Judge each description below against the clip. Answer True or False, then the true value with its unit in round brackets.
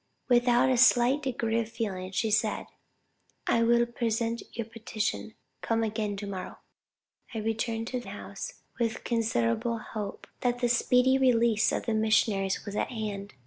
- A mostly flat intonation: True (2.0 semitones)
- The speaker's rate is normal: True (155 wpm)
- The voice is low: False (225 Hz)